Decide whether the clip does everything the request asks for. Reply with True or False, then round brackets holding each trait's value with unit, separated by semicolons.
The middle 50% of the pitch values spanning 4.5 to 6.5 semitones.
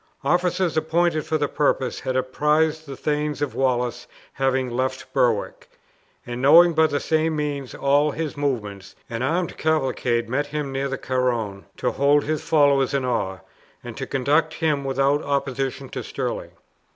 False (3.0 semitones)